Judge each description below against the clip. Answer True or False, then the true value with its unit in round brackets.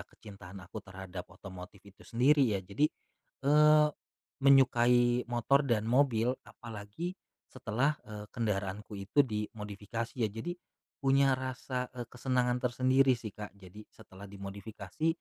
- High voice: False (115 Hz)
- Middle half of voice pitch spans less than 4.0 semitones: False (4.4 semitones)